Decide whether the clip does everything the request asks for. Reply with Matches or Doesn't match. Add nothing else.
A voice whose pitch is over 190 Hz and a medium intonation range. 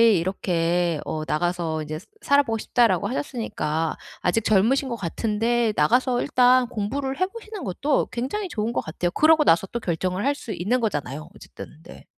Doesn't match